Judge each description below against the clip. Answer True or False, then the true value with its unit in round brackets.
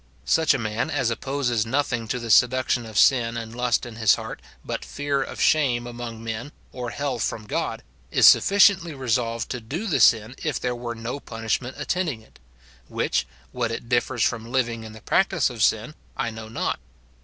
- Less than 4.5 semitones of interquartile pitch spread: True (2.9 semitones)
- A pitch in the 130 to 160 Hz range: False (120 Hz)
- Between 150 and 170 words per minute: False (190 wpm)